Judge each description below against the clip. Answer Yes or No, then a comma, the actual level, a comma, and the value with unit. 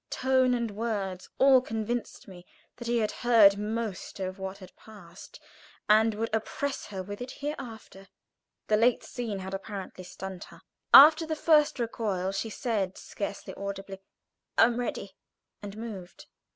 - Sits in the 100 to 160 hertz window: No, high, 215 Hz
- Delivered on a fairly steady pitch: No, average, 3.6 semitones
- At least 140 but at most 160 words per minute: Yes, average, 150 wpm